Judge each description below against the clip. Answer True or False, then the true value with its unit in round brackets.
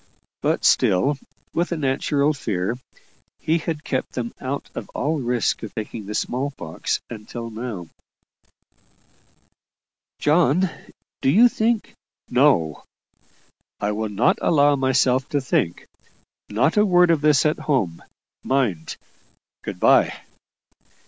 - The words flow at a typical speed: False (125 wpm)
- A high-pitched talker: False (130 Hz)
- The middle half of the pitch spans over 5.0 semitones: True (5.6 semitones)